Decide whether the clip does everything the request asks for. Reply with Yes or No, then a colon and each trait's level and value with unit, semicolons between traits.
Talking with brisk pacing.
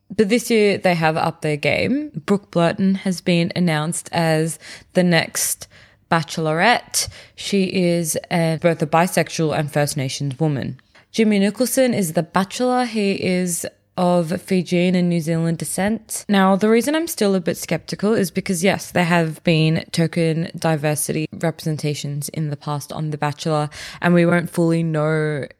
No: average, 160 wpm